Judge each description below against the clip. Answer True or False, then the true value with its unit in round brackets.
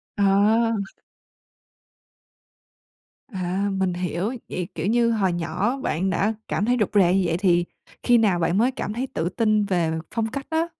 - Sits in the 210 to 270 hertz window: False (200 Hz)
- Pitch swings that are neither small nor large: True (4.3 semitones)